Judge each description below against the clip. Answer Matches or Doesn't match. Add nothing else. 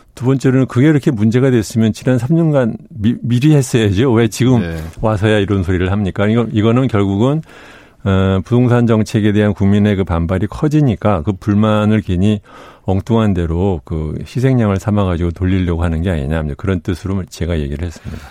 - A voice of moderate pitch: Doesn't match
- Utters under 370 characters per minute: Doesn't match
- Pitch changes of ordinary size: Matches